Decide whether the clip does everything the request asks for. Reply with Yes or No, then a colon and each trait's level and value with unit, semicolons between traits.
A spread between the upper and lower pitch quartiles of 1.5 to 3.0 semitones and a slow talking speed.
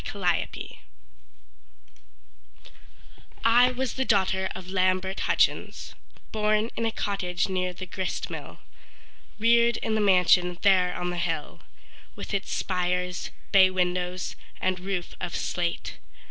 Yes: average, 2.7 semitones; slow, 125 wpm